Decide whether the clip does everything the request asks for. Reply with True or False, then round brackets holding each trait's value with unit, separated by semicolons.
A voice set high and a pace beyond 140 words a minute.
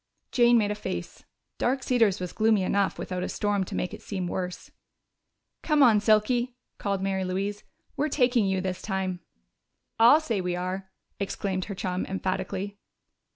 True (200 Hz; 160 wpm)